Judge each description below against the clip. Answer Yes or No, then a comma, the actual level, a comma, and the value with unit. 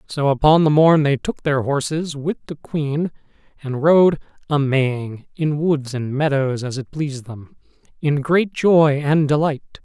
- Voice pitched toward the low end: No, medium, 145 Hz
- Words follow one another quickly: No, average, 170 wpm